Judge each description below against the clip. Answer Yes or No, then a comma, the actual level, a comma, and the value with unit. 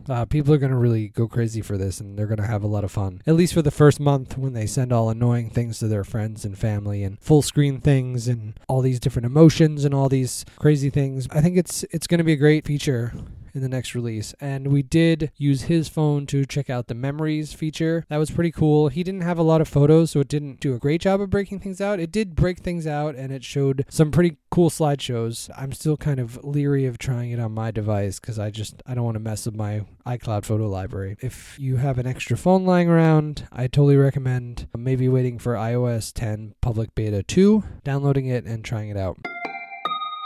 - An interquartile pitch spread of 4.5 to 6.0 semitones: Yes, average, 4.9 semitones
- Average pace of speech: No, fast, 235 wpm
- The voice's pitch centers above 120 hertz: Yes, low, 135 Hz